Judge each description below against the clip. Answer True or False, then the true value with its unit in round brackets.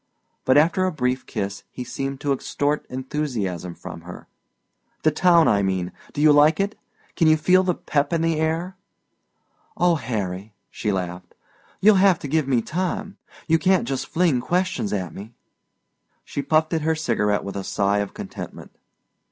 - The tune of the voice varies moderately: False (7.8 semitones)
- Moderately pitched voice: True (145 Hz)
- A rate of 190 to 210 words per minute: False (170 wpm)